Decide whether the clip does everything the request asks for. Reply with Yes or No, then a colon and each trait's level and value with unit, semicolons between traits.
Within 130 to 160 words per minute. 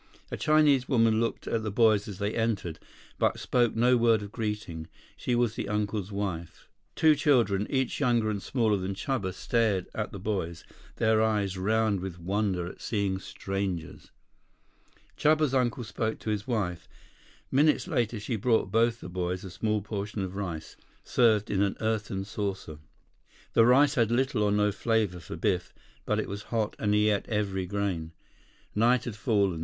No: average, 170 wpm